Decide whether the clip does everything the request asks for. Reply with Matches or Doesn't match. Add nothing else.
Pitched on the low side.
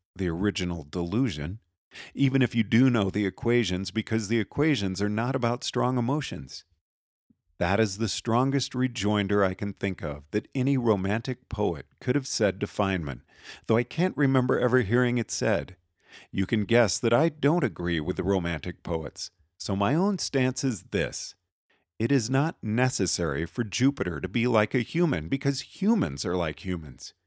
Matches